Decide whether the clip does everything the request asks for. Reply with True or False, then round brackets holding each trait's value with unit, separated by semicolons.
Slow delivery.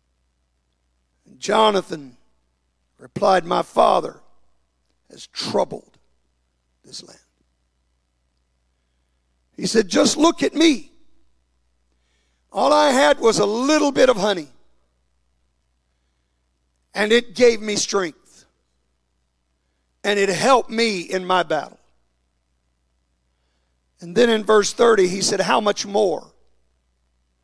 True (100 wpm)